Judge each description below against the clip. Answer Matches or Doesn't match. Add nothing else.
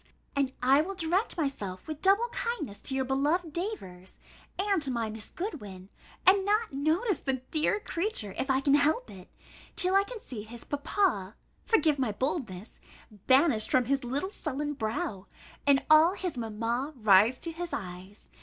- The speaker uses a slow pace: Doesn't match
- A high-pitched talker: Matches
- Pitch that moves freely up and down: Matches